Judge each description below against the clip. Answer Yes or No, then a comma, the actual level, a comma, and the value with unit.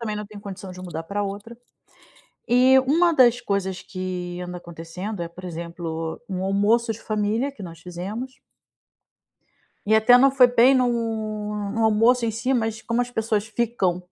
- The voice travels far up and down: No, average, 4.4 semitones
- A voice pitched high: Yes, high, 215 Hz